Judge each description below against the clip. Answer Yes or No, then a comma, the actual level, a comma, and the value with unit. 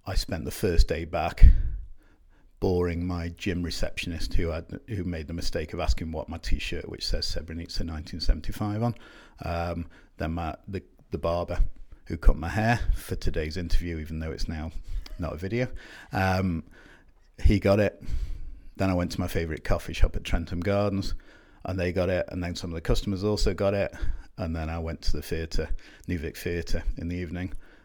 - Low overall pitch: Yes, very low, 85 Hz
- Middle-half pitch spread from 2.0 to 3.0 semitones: Yes, narrow, 2.5 semitones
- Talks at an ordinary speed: Yes, average, 185 wpm